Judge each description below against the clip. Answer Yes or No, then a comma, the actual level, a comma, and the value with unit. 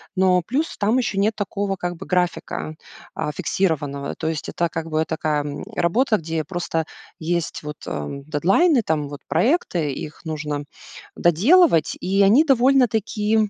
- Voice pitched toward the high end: No, medium, 175 Hz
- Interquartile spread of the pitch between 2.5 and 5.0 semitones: No, wide, 5.5 semitones